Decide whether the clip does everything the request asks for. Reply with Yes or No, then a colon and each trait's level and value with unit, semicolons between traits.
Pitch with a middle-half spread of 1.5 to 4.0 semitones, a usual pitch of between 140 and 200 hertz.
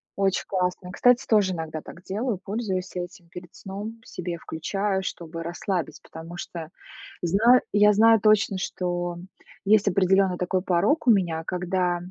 Yes: average, 2.8 semitones; medium, 185 Hz